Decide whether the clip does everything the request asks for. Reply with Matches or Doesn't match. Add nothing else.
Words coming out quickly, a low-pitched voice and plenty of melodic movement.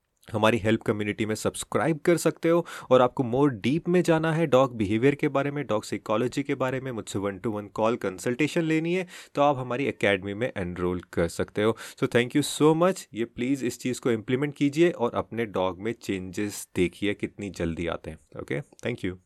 Matches